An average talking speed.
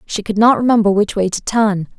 No: fast, 240 wpm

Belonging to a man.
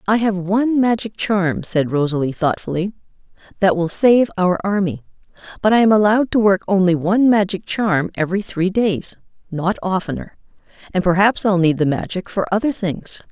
No: female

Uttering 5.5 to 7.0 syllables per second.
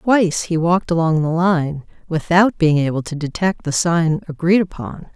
No: 4.8 syllables/s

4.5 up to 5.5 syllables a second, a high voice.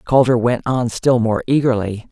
No: 4.8 syllables/s; low, 120 Hz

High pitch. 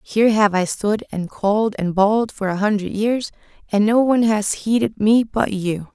Yes: high, 210 Hz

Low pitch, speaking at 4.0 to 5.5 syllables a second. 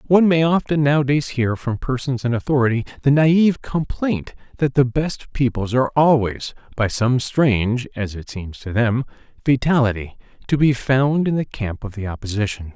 Yes: low, 130 Hz; 5.0 syllables/s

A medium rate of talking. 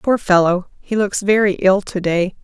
Yes: average, 195 wpm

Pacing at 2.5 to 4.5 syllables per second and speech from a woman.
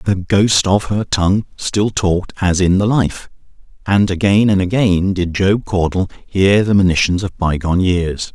No: 4.4 syllables/s; male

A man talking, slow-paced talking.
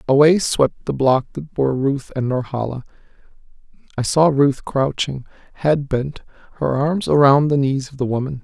No: male; average, 165 wpm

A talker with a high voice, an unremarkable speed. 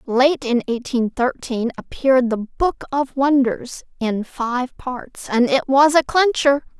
Yes: very high, 260 Hz; average, 150 wpm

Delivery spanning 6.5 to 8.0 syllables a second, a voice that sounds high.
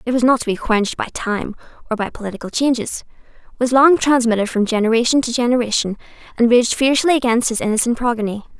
Yes: 6.6 syllables/s; high, 235 Hz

